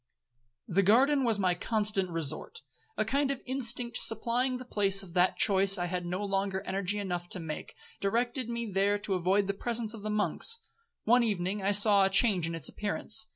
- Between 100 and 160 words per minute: No, average, 190 wpm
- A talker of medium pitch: No, high, 205 Hz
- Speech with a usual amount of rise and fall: Yes, average, 3.7 semitones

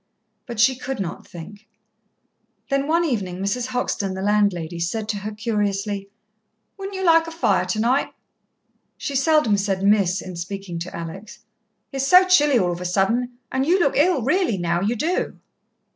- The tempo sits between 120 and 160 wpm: No, average, 170 wpm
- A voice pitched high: Yes, high, 215 Hz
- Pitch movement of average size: No, wide, 6.1 semitones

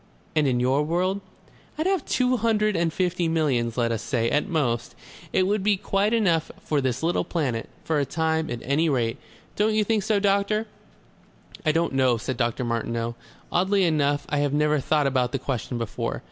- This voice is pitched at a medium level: Yes, medium, 155 Hz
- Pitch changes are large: Yes, wide, 7.1 semitones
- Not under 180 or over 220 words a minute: Yes, average, 190 wpm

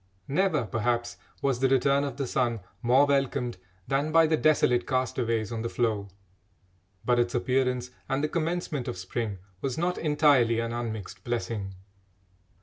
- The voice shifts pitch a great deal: No, average, 3.2 semitones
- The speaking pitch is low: Yes, low, 125 Hz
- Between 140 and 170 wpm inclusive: Yes, average, 150 wpm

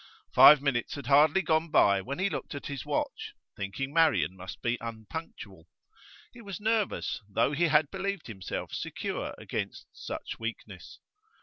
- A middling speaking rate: Yes, average, 150 wpm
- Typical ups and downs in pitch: No, wide, 6.7 semitones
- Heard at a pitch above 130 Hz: Yes, medium, 140 Hz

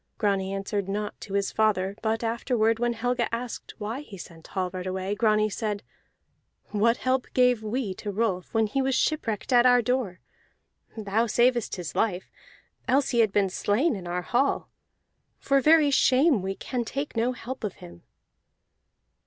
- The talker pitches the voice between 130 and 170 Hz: No, high, 220 Hz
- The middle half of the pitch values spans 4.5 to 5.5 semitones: No, average, 4.0 semitones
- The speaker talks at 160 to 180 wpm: Yes, average, 165 wpm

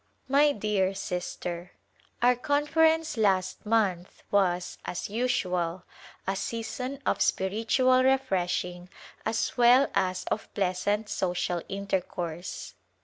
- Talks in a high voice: Yes, high, 200 Hz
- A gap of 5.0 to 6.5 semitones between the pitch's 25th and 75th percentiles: Yes, wide, 5.5 semitones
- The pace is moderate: No, slow, 100 wpm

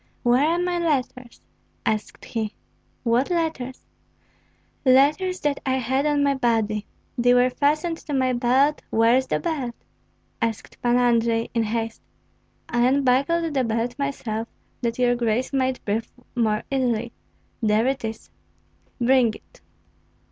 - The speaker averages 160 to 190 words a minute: No, average, 140 wpm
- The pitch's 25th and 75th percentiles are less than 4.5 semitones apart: Yes, average, 3.2 semitones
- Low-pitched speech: No, very high, 250 Hz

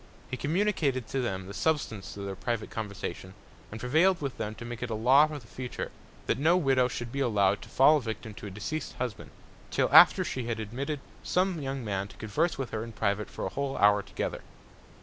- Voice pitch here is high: No, low, 120 Hz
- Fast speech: Yes, fast, 220 wpm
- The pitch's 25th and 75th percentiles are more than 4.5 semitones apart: Yes, average, 4.9 semitones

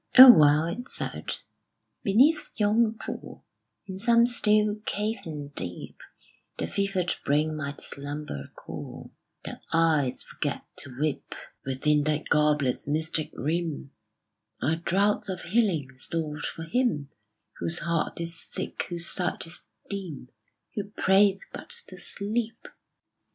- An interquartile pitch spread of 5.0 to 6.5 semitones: Yes, wide, 5.5 semitones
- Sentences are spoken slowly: Yes, slow, 125 wpm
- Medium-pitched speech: Yes, medium, 170 Hz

